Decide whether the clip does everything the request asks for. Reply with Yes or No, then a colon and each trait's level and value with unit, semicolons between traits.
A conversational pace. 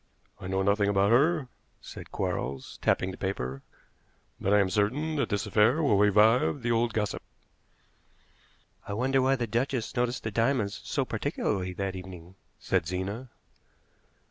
Yes: average, 150 wpm